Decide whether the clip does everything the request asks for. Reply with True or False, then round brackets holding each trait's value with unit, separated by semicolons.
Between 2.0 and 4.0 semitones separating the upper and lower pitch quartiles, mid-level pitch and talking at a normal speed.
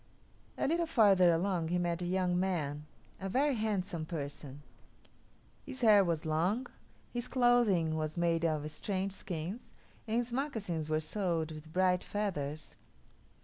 False (5.0 semitones; 180 Hz; 145 wpm)